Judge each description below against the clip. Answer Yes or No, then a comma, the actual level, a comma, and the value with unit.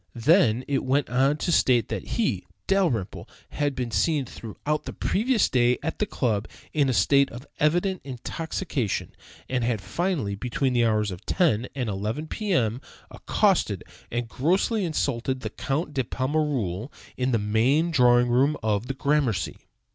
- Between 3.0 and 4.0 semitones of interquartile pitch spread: No, average, 4.7 semitones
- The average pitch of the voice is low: Yes, low, 130 Hz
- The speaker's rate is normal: Yes, average, 160 wpm